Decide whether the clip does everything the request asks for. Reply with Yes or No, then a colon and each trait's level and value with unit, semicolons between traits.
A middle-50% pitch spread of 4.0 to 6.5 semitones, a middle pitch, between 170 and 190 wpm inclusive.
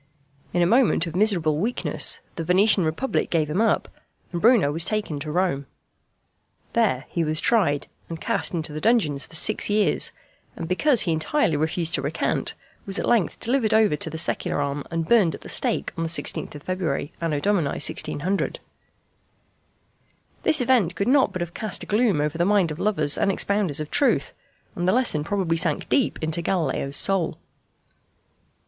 Yes: average, 5.2 semitones; medium, 175 Hz; average, 175 wpm